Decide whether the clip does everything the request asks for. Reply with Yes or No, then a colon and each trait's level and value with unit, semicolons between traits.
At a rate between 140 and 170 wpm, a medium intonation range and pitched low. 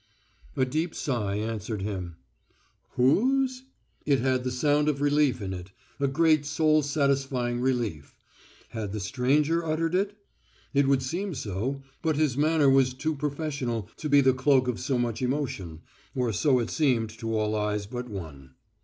Yes: average, 160 wpm; average, 4.8 semitones; low, 130 Hz